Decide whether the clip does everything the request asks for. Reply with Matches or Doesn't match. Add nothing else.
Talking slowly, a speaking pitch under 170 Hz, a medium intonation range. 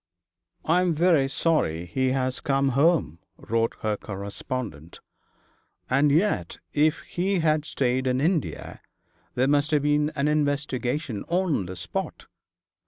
Matches